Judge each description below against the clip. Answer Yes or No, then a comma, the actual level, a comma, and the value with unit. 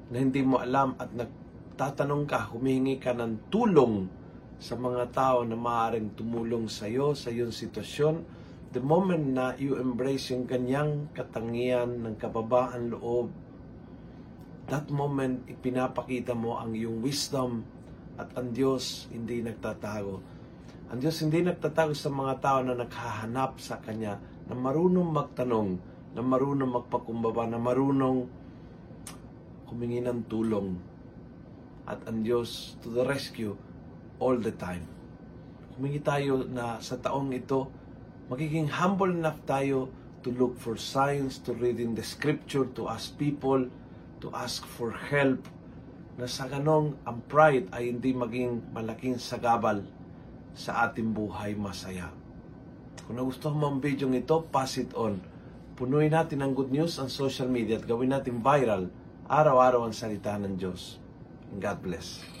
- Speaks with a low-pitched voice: Yes, low, 125 Hz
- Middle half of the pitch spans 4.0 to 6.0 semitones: No, average, 2.9 semitones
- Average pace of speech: Yes, average, 140 wpm